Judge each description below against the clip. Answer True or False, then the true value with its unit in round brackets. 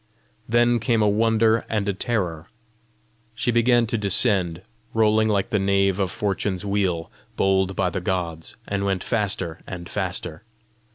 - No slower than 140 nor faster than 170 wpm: True (150 wpm)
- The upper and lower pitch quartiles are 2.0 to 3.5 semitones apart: True (3.1 semitones)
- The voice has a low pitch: True (100 Hz)